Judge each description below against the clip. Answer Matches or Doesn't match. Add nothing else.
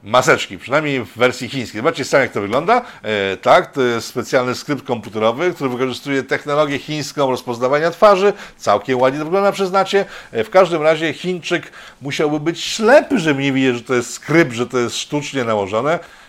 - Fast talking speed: Matches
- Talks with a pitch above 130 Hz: Matches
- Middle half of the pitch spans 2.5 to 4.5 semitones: Doesn't match